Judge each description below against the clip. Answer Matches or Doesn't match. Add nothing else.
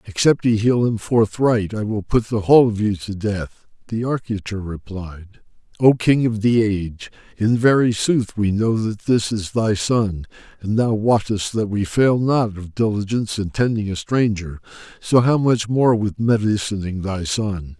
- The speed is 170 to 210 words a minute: Matches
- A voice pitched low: Matches